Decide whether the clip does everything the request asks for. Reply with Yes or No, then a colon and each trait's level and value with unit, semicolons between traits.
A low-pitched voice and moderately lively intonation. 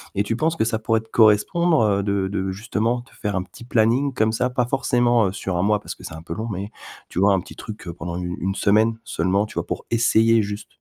Yes: low, 110 Hz; average, 3.1 semitones